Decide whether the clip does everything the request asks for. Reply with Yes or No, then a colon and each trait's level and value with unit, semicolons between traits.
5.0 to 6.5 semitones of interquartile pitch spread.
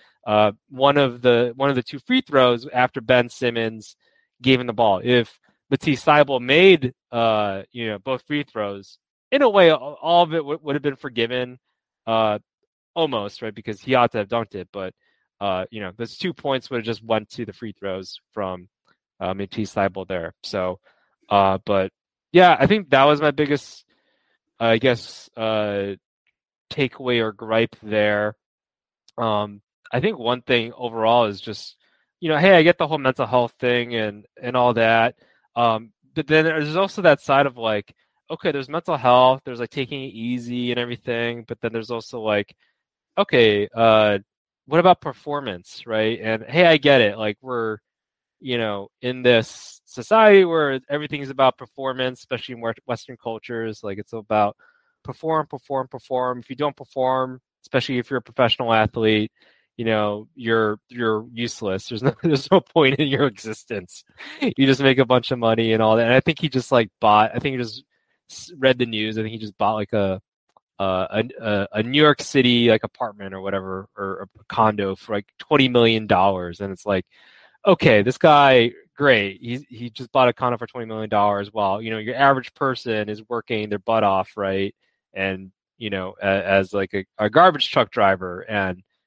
No: average, 3.9 semitones